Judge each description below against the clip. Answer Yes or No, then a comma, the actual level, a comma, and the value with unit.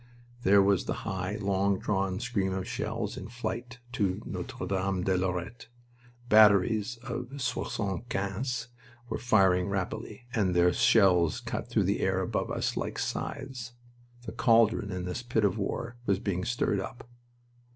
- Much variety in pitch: No, average, 3.5 semitones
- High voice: No, low, 100 Hz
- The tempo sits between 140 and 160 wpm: Yes, average, 150 wpm